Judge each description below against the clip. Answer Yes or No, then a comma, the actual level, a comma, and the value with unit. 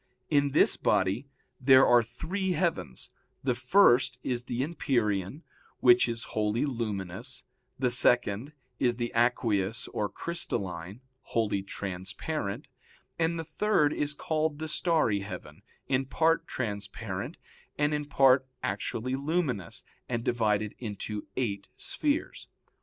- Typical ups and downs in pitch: No, wide, 5.8 semitones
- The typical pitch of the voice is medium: No, low, 125 Hz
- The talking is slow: Yes, slow, 120 wpm